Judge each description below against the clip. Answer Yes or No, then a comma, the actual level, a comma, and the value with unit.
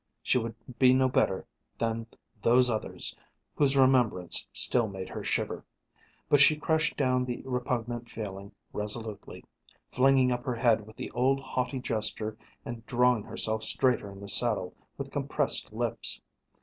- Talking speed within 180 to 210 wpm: No, average, 150 wpm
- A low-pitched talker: Yes, low, 120 Hz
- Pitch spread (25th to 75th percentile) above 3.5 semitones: No, average, 2.8 semitones